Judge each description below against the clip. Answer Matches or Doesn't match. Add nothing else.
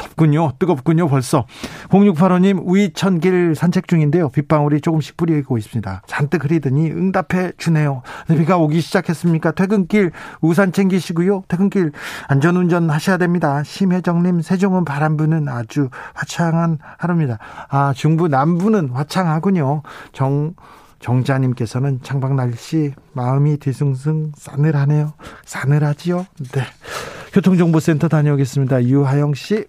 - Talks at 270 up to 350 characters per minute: Matches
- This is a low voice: Doesn't match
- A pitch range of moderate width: Matches